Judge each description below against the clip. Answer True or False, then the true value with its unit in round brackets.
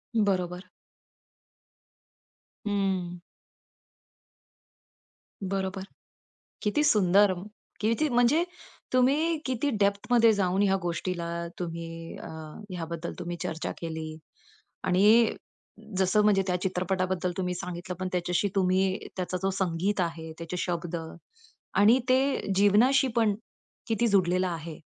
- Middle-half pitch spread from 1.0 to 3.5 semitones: True (3.1 semitones)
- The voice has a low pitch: False (190 Hz)